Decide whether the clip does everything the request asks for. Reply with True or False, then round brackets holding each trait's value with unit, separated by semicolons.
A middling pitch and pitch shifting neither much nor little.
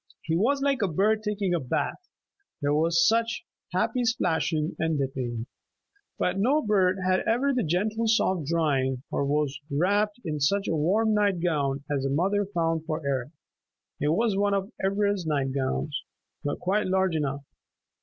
False (175 Hz; 5.9 semitones)